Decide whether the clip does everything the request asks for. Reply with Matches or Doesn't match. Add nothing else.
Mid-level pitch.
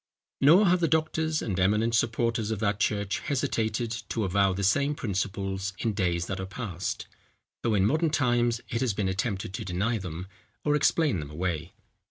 Doesn't match